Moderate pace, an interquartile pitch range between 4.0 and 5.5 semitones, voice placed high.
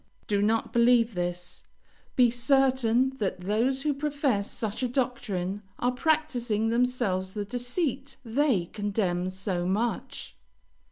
No: slow, 120 wpm; average, 4.5 semitones; high, 235 Hz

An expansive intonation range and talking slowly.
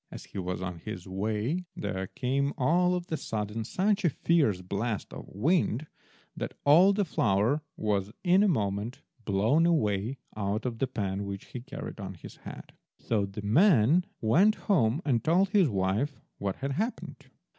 No: wide, 8.5 semitones; average, 170 wpm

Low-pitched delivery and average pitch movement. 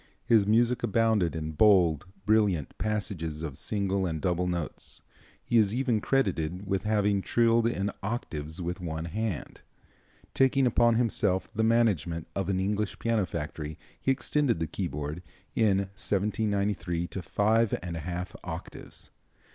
Yes: low, 100 Hz; average, 4.5 semitones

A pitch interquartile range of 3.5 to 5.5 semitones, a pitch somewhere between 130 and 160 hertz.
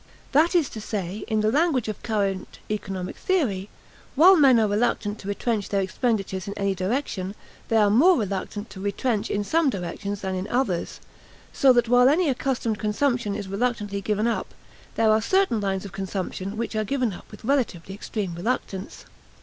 No: average, 4.0 semitones; high, 215 Hz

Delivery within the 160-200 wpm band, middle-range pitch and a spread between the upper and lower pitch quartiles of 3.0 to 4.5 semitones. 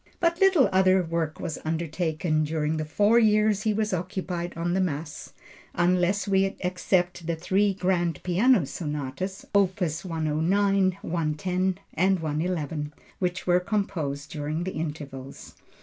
No: slow, 135 wpm; medium, 180 Hz; average, 3.4 semitones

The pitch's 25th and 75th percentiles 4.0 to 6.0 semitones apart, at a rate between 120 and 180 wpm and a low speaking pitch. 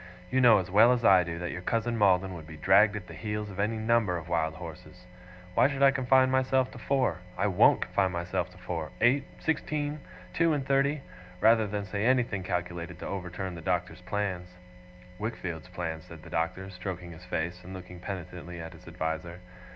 No: average, 4.5 semitones; average, 195 wpm; very low, 95 Hz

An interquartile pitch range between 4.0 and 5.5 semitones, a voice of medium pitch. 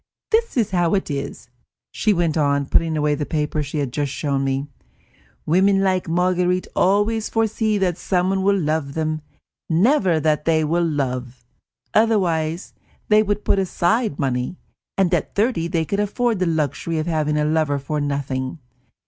Yes: average, 4.7 semitones; medium, 165 Hz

